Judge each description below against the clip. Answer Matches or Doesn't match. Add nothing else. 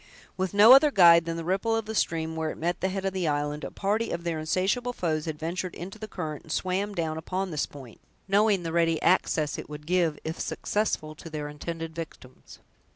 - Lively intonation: Doesn't match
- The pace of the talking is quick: Matches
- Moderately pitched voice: Matches